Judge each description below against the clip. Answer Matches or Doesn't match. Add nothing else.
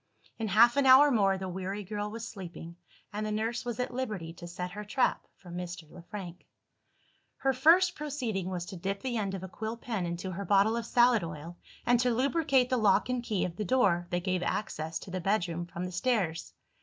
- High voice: Matches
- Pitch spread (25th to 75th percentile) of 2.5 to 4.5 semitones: Doesn't match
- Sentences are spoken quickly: Matches